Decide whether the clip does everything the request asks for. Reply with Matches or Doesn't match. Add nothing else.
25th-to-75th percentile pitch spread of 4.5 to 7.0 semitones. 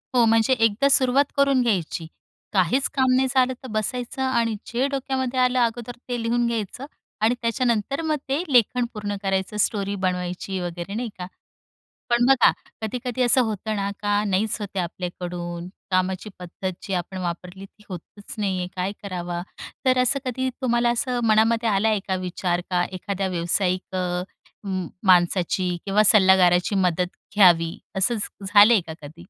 Matches